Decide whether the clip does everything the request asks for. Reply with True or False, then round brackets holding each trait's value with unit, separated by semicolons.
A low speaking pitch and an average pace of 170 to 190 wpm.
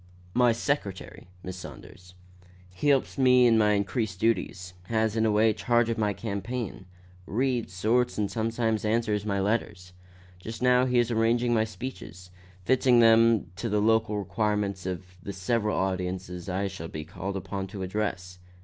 False (105 Hz; 160 wpm)